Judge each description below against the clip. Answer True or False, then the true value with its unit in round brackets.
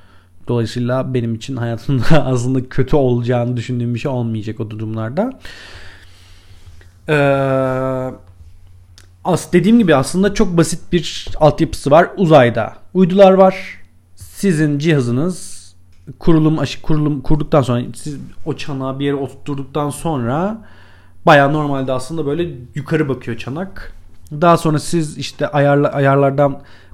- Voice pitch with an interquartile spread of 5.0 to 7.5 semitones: True (5.6 semitones)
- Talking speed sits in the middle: True (115 wpm)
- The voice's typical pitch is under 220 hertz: True (135 Hz)